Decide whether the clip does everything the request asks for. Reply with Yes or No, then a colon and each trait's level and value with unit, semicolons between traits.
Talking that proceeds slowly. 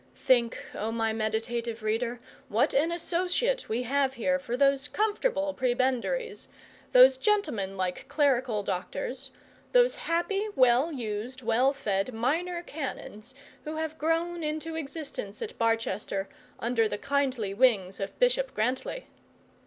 Yes: slow, 125 wpm